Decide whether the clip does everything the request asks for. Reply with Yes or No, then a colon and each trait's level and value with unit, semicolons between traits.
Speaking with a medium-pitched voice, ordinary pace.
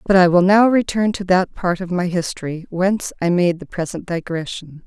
No: medium, 180 Hz; fast, 210 wpm